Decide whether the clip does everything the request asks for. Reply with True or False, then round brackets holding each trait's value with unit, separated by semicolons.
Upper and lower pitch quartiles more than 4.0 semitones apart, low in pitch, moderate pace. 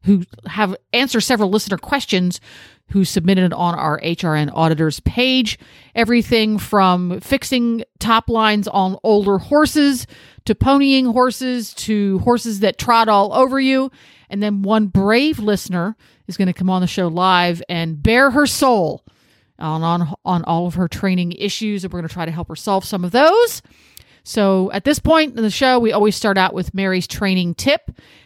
False (4.7 semitones; 200 Hz; 175 wpm)